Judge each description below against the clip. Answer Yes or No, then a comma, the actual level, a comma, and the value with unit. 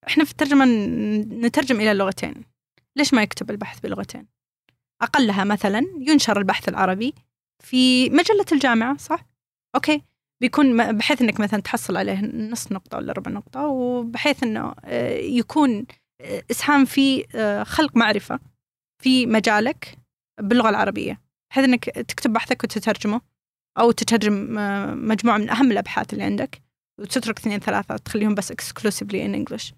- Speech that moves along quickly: No, average, 125 wpm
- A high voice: Yes, high, 235 Hz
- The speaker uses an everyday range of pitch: Yes, average, 4.2 semitones